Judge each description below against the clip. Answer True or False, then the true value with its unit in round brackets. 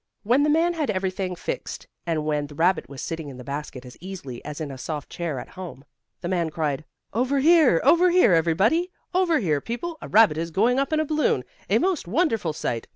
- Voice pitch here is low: False (185 Hz)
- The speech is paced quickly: True (220 wpm)